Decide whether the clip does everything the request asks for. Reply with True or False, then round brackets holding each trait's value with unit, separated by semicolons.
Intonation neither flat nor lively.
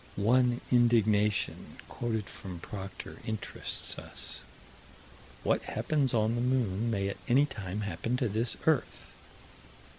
True (3.3 semitones)